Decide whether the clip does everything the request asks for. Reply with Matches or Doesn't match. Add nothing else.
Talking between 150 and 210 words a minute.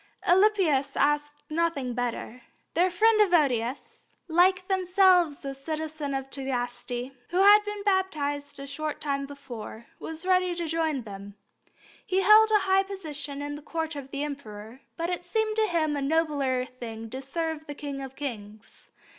Matches